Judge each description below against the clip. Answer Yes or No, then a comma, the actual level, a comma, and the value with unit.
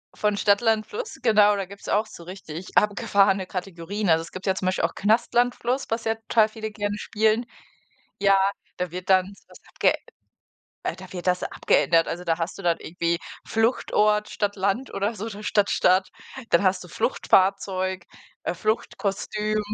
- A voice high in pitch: Yes, high, 200 Hz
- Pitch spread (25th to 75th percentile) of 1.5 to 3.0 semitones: Yes, average, 2.7 semitones